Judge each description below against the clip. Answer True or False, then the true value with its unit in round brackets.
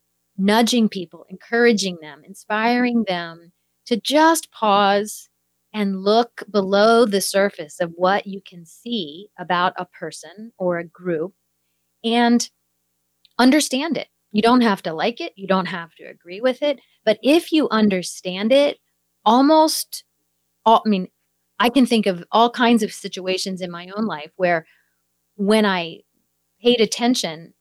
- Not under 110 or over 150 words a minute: True (145 wpm)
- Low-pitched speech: False (195 Hz)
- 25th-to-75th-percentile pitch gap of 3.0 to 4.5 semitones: False (5.5 semitones)